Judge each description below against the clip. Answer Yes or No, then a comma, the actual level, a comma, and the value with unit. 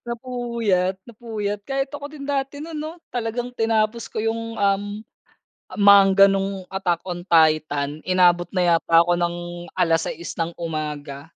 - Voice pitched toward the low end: No, high, 195 Hz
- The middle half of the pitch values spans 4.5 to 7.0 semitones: Yes, wide, 5.4 semitones